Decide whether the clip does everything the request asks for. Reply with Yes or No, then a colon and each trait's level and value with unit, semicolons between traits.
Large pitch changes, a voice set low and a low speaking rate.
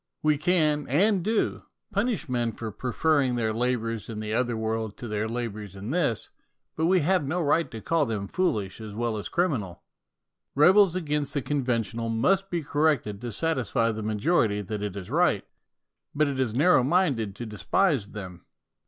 No: wide, 6.5 semitones; low, 125 Hz; average, 175 wpm